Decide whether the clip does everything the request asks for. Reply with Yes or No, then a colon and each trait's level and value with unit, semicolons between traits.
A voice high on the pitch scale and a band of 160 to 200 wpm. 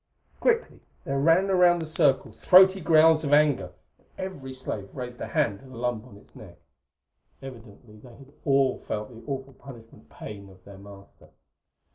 No: low, 130 Hz; average, 170 wpm